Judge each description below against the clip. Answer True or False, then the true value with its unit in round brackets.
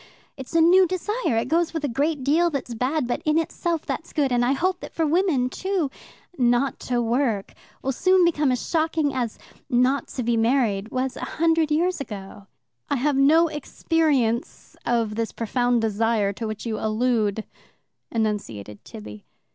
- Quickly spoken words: False (170 wpm)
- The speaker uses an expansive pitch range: True (5.8 semitones)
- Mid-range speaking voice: False (260 Hz)